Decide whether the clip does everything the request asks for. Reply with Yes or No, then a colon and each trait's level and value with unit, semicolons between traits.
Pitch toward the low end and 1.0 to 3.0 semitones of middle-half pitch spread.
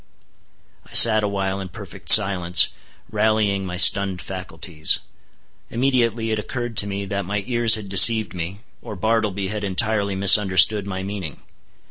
Yes: low, 100 Hz; narrow, 2.4 semitones